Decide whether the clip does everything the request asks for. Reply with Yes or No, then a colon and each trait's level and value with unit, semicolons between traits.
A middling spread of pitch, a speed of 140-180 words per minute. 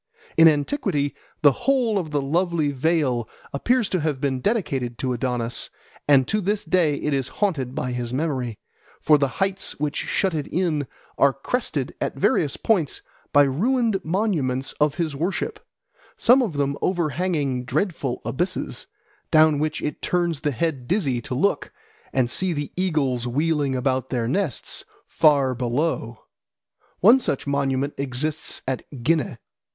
Yes: average, 4.9 semitones; average, 150 wpm